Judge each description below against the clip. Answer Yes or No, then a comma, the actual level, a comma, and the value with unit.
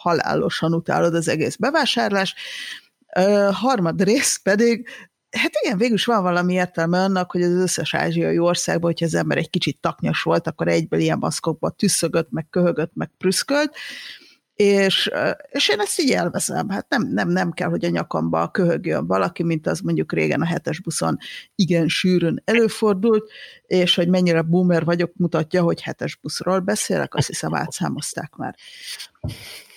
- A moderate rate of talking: No, fast, 160 wpm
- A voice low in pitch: No, medium, 180 Hz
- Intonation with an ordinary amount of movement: Yes, average, 3.9 semitones